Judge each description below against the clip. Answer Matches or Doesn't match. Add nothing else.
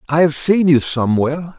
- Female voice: Doesn't match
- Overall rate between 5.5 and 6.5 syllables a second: Matches